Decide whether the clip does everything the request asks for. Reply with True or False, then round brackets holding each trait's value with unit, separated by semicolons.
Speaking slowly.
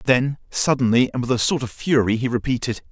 False (205 wpm)